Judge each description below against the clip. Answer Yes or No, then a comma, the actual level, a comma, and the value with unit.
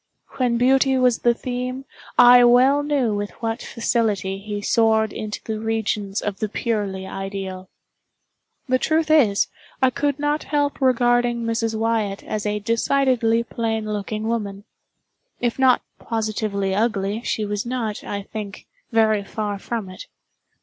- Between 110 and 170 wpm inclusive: Yes, average, 145 wpm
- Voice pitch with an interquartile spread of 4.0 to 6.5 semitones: No, average, 3.0 semitones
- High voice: Yes, high, 225 Hz